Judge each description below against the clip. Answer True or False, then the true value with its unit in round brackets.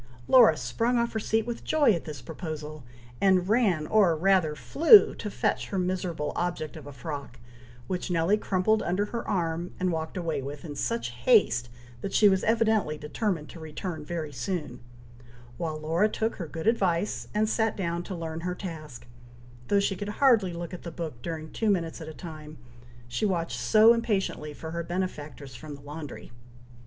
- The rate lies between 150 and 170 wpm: False (185 wpm)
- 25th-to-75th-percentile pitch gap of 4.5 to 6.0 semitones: True (4.9 semitones)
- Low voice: False (170 Hz)